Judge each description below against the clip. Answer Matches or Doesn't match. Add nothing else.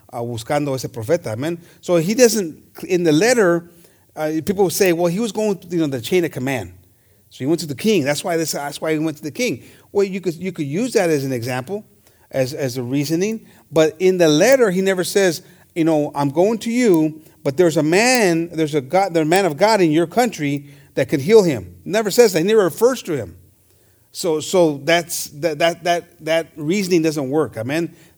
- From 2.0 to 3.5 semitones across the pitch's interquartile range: Doesn't match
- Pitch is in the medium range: Matches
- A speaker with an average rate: Doesn't match